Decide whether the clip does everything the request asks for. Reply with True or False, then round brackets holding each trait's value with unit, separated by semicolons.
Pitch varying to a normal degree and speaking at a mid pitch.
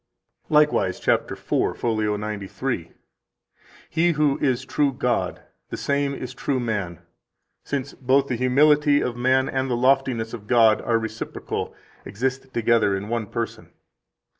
False (3.4 semitones; 125 Hz)